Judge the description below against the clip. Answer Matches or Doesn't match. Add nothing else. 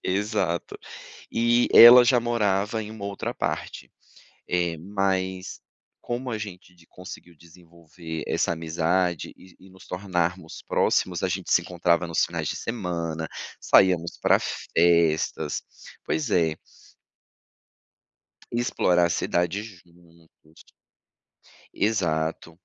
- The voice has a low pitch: Matches